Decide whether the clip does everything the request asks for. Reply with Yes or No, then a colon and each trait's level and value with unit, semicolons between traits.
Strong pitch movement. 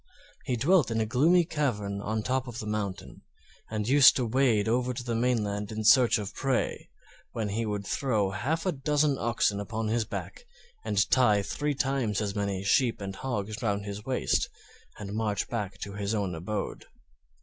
No: average, 3.9 semitones